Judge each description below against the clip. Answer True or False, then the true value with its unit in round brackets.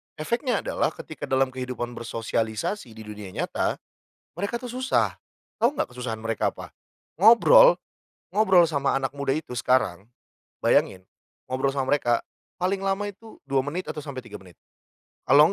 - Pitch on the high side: False (140 Hz)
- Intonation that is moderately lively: False (8.3 semitones)